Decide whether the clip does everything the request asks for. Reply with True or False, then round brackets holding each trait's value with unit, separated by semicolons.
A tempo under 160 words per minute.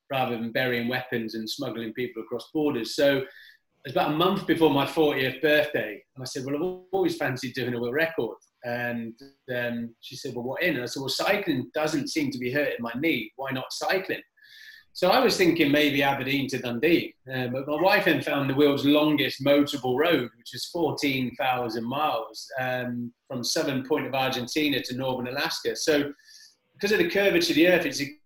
False (200 wpm)